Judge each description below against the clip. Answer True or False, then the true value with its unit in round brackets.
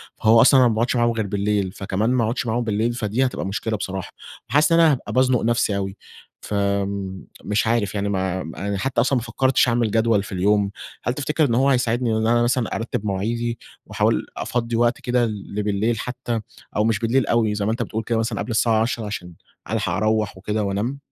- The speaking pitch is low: True (110 Hz)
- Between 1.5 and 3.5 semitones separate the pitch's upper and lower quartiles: True (2.8 semitones)